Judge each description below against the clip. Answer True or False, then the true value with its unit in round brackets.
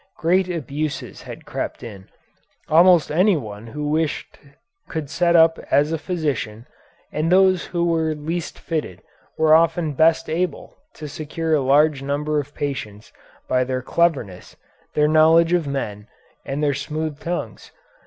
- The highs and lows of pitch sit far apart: False (3.0 semitones)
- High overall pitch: False (155 Hz)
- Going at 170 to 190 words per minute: False (145 wpm)